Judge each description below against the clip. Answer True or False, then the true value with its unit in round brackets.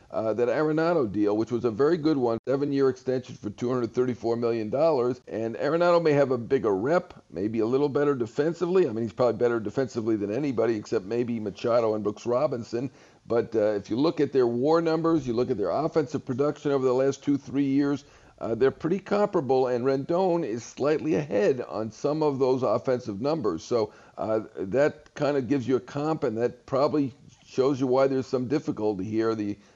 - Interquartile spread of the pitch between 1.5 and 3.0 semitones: False (3.8 semitones)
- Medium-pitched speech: False (130 Hz)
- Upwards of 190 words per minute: True (200 wpm)